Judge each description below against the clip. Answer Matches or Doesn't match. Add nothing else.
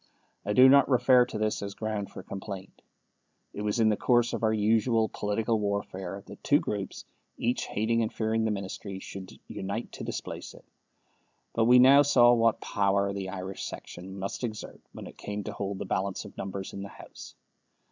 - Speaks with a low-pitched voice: Matches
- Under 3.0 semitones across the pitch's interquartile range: Matches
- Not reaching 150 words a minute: Doesn't match